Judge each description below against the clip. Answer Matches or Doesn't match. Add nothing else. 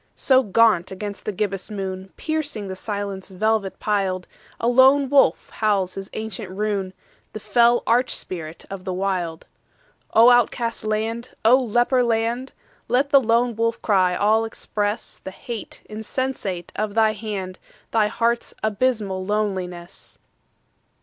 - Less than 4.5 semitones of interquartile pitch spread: Matches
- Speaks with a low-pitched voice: Doesn't match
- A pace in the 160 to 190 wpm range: Doesn't match